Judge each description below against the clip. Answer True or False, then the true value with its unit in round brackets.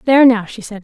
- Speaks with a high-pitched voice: True (225 Hz)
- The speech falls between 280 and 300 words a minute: True (285 wpm)